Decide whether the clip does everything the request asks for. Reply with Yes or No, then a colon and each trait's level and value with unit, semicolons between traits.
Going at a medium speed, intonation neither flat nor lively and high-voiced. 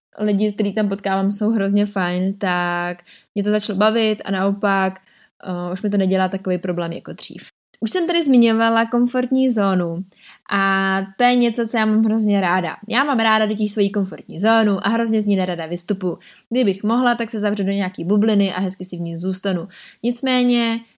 No: fast, 190 wpm; average, 3.0 semitones; high, 205 Hz